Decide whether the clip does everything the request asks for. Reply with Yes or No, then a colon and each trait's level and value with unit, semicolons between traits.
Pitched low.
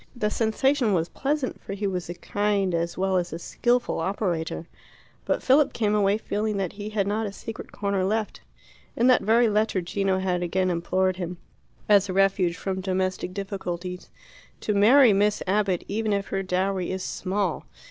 No: high, 195 Hz